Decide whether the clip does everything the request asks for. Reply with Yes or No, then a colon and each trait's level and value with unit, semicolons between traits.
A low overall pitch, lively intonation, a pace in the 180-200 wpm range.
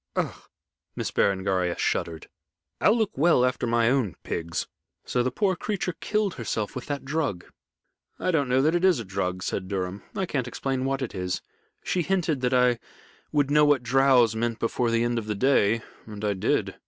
Yes: low, 125 Hz; wide, 5.7 semitones; average, 190 wpm